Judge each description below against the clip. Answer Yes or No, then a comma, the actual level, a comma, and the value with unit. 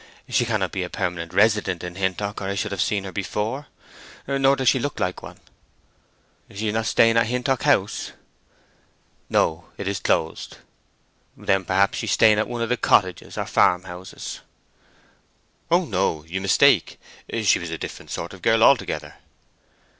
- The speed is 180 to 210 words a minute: No, average, 165 wpm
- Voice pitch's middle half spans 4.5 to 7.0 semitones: No, average, 4.0 semitones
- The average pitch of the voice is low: Yes, low, 100 Hz